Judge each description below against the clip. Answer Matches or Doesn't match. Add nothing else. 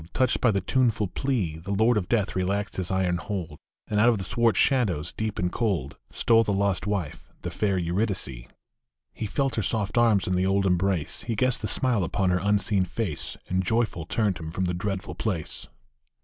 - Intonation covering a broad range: Doesn't match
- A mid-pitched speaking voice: Doesn't match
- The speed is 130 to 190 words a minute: Doesn't match